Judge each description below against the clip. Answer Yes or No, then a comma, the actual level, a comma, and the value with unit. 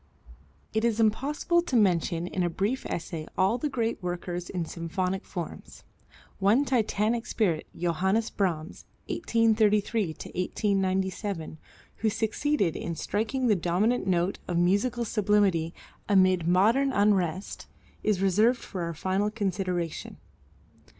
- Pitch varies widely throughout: No, average, 4.0 semitones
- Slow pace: Yes, slow, 120 wpm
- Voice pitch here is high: Yes, high, 195 Hz